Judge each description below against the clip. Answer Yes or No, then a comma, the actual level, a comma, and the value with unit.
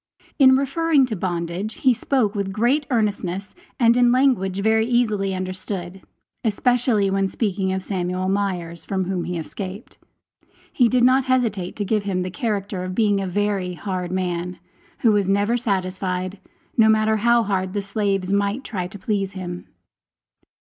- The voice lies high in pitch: Yes, high, 200 Hz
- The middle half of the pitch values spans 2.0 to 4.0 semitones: Yes, average, 3.4 semitones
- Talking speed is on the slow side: No, average, 160 wpm